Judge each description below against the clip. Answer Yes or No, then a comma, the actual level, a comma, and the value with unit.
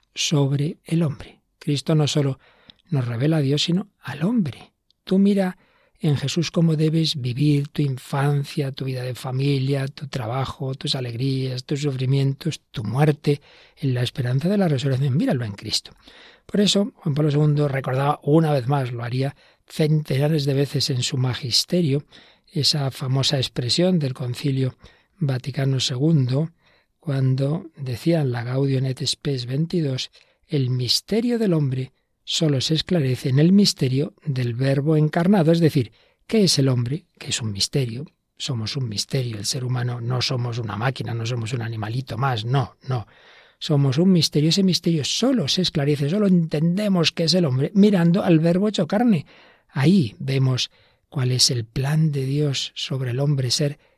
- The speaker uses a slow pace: No, average, 160 wpm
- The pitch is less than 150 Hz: Yes, medium, 140 Hz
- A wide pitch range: No, average, 3.4 semitones